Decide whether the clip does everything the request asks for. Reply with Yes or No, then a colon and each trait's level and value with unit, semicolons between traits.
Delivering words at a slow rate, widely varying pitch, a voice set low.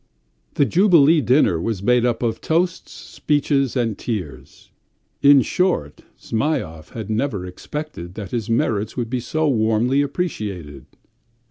Yes: slow, 130 wpm; wide, 5.8 semitones; low, 120 Hz